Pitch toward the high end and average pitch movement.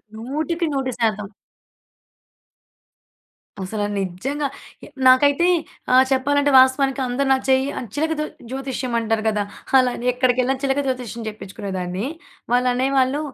Yes: very high, 260 Hz; average, 3.5 semitones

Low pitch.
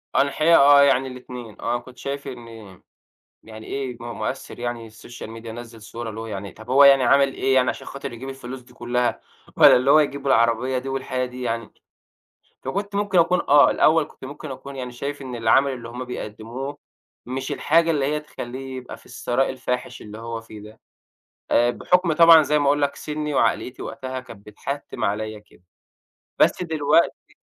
Yes: low, 130 Hz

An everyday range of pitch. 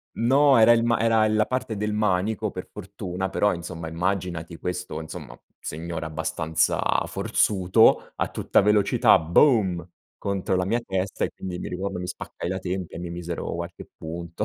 Yes: average, 3.6 semitones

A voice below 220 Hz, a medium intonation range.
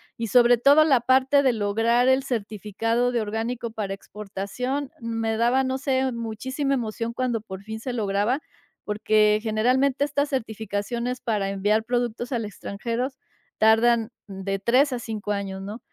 No: high, 230 Hz; average, 3.1 semitones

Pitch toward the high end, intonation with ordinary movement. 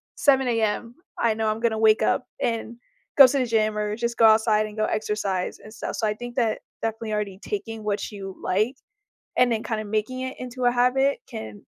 No: high, 220 Hz; narrow, 2.3 semitones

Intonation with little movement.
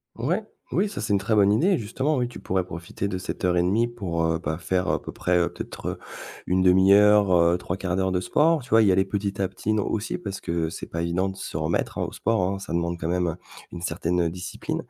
No: average, 3.2 semitones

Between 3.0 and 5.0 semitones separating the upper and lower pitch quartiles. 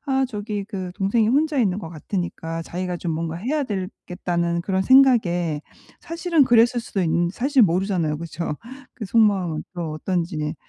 No: wide, 5.4 semitones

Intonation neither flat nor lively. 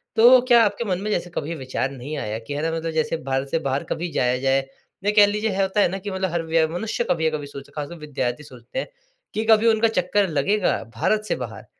No: wide, 6.8 semitones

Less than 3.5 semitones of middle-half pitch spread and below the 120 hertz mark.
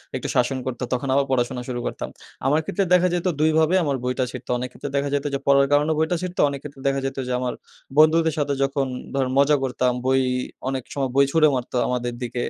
No: average, 2.9 semitones; low, 135 Hz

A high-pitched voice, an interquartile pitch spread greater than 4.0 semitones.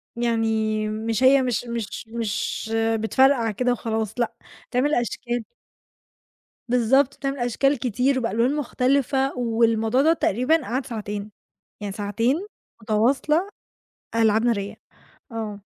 No: high, 235 Hz; average, 3.1 semitones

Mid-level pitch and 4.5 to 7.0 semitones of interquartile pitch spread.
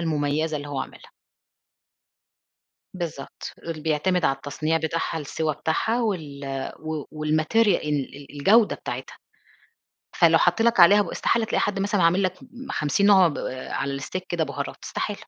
Yes: medium, 160 Hz; average, 5.0 semitones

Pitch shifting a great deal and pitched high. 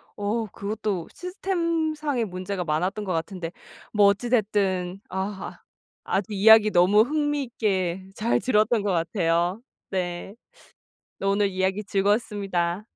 No: average, 3.2 semitones; high, 200 Hz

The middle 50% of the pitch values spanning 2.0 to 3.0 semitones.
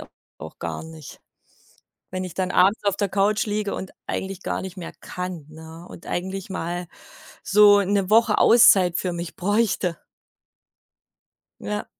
Yes: narrow, 2.5 semitones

